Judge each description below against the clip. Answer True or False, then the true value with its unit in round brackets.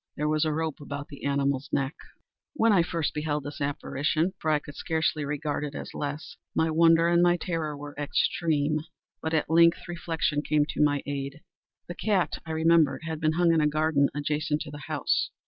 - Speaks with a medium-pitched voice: True (155 Hz)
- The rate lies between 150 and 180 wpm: False (190 wpm)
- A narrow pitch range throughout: True (2.1 semitones)